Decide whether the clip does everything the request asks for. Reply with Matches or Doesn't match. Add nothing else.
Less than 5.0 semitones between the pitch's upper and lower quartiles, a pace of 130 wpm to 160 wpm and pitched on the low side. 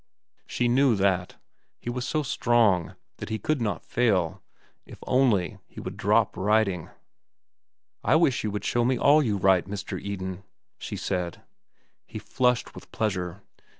Matches